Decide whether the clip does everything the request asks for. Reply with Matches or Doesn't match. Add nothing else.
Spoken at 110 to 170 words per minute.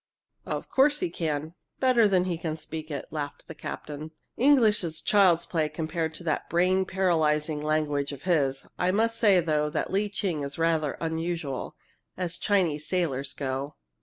Matches